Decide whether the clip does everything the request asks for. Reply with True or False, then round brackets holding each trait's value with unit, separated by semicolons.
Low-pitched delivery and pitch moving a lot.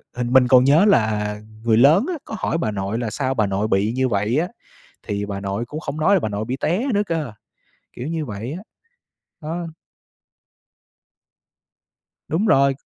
True (125 Hz; 6.8 semitones)